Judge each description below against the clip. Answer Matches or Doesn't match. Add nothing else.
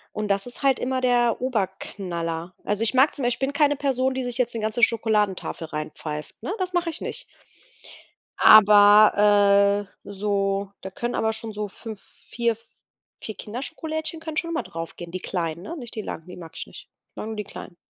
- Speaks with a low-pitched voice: Doesn't match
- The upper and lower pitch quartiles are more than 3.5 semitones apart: Matches